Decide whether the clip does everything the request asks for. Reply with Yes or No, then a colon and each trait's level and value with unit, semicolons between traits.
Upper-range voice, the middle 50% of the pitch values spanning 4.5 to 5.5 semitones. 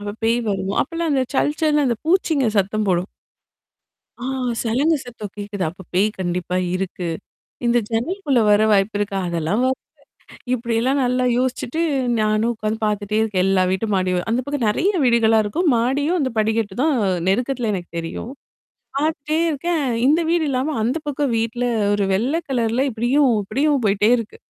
Yes: high, 230 Hz; average, 5.2 semitones